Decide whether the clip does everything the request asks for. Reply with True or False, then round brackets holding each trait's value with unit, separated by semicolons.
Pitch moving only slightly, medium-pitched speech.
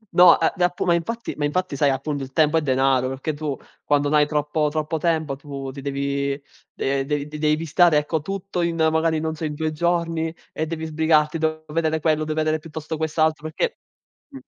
True (1.7 semitones; 155 Hz)